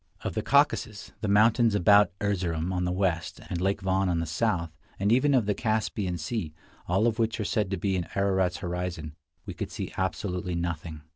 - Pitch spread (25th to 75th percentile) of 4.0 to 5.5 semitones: No, average, 3.3 semitones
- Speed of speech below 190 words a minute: No, average, 200 wpm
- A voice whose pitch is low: Yes, very low, 95 Hz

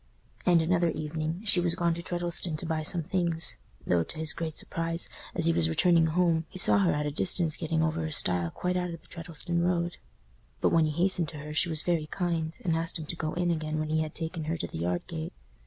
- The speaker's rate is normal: No, fast, 245 wpm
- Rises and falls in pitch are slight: Yes, narrow, 1.8 semitones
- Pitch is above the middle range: No, medium, 165 Hz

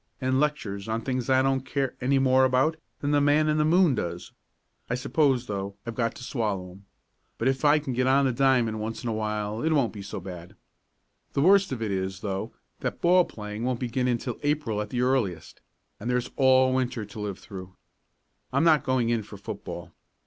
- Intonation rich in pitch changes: No, average, 4.3 semitones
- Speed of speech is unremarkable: No, fast, 210 wpm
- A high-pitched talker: No, low, 125 Hz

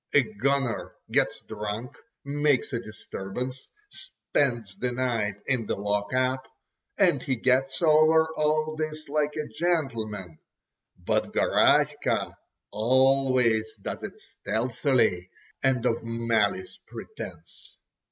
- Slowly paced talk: Yes, slow, 105 wpm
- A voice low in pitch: Yes, low, 130 Hz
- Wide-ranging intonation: No, average, 4.5 semitones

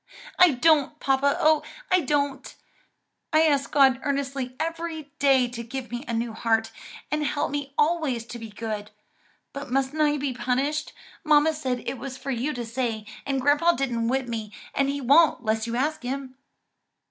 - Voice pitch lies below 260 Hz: No, very high, 270 Hz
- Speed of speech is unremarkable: Yes, average, 175 wpm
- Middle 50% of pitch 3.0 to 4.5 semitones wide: Yes, average, 3.4 semitones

